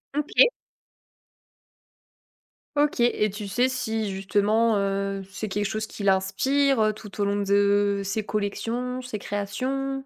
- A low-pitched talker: No, high, 215 Hz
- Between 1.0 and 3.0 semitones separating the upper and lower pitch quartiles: No, average, 3.8 semitones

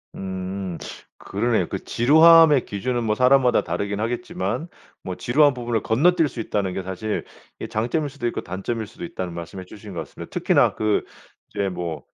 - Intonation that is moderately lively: No, wide, 6.0 semitones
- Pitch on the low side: Yes, low, 110 Hz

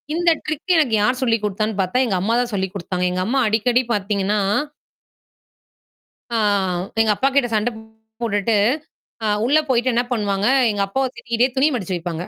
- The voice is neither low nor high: No, high, 225 Hz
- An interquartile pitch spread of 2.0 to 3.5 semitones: No, average, 4.0 semitones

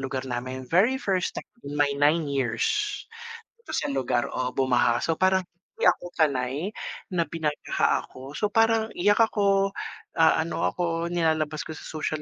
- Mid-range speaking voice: Yes, medium, 155 Hz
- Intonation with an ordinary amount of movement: No, wide, 5.7 semitones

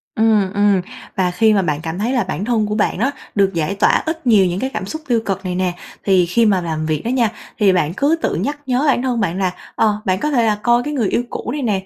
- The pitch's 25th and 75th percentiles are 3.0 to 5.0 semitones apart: Yes, average, 4.4 semitones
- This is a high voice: Yes, high, 210 Hz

